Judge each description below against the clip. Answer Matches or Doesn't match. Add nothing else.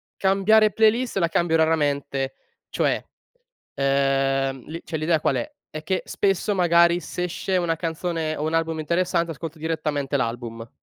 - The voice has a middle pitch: Matches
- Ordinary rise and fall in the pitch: Matches